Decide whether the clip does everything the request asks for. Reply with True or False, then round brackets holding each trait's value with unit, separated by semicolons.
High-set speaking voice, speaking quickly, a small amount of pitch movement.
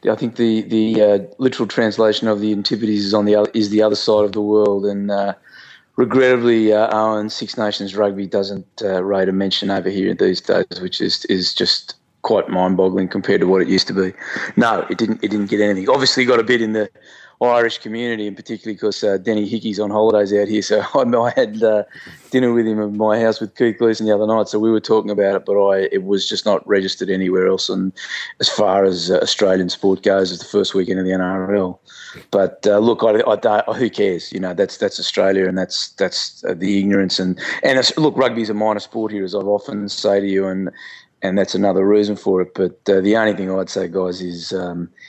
False (105 Hz; 235 wpm; 2.3 semitones)